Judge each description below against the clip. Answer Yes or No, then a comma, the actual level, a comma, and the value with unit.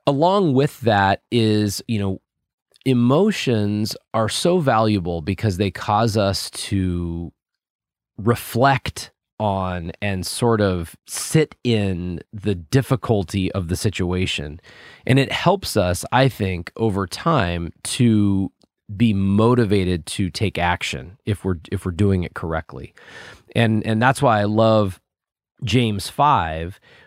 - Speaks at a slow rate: Yes, slow, 125 wpm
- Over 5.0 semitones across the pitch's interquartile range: No, average, 4.0 semitones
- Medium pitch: No, low, 105 Hz